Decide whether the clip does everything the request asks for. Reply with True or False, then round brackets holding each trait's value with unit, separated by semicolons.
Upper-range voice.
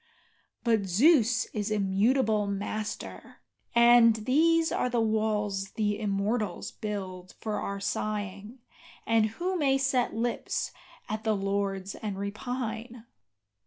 True (215 Hz)